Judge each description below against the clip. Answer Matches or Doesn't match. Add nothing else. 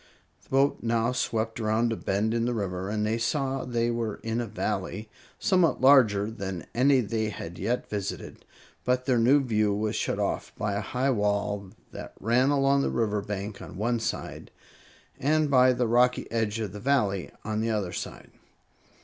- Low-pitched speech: Matches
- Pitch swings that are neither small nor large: Matches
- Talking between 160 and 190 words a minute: Matches